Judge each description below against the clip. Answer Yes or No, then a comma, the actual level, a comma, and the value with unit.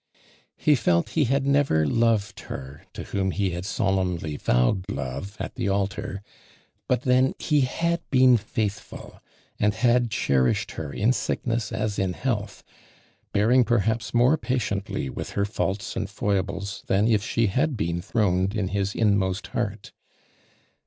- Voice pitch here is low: Yes, low, 105 Hz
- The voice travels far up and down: No, average, 3.9 semitones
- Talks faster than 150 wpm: No, average, 145 wpm